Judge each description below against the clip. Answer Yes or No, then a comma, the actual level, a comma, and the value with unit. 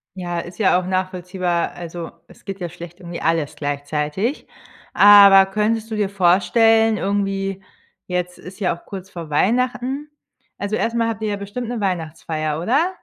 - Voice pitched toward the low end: No, high, 190 Hz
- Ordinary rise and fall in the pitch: Yes, average, 3.7 semitones